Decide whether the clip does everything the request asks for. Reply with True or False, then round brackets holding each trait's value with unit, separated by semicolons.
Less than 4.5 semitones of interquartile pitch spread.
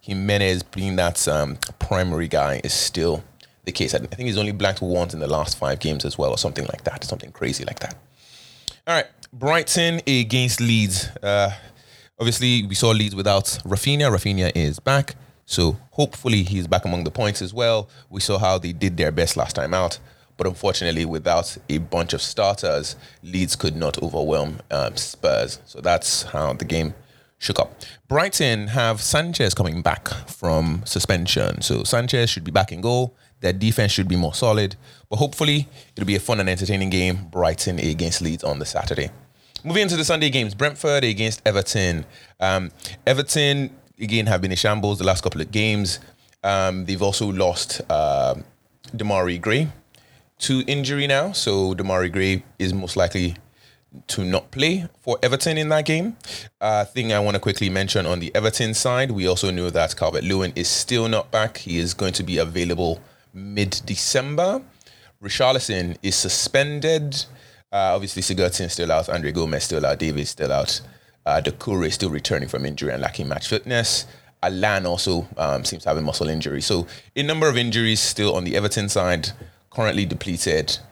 False (5.3 semitones)